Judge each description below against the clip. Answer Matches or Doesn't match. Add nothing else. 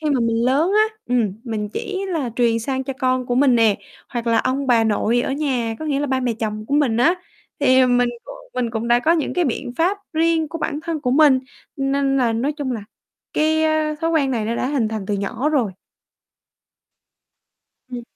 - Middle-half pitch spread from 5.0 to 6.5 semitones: Doesn't match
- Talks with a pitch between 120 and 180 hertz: Doesn't match